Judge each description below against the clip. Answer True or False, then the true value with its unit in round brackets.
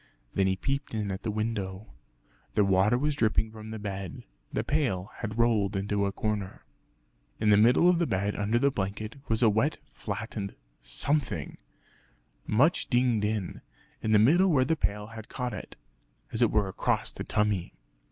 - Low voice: True (110 Hz)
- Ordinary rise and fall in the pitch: True (3.3 semitones)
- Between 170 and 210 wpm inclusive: True (175 wpm)